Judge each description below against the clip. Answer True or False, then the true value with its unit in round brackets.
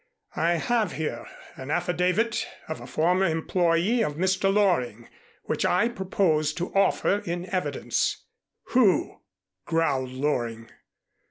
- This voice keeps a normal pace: False (115 wpm)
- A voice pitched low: False (175 Hz)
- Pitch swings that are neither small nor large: True (4.1 semitones)